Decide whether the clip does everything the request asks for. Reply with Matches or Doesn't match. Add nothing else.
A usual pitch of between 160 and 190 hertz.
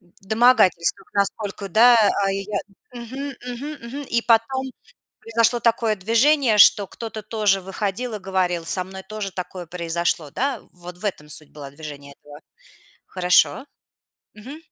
Doesn't match